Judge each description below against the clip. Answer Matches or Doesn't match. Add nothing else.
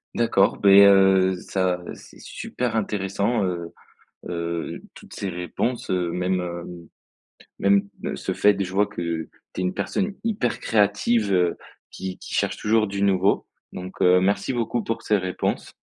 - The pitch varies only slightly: Matches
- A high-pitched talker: Doesn't match